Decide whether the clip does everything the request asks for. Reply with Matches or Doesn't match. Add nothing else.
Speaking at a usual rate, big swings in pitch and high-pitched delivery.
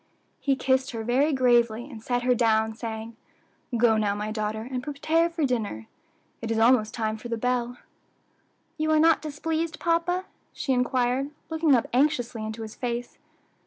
Doesn't match